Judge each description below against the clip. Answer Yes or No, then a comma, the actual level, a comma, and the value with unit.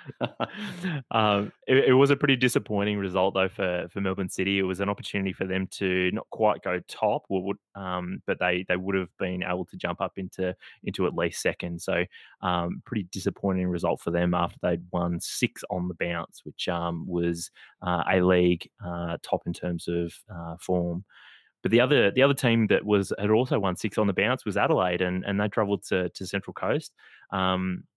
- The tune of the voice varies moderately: No, narrow, 2.3 semitones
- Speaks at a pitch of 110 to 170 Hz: No, very low, 95 Hz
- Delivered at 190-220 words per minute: Yes, average, 200 wpm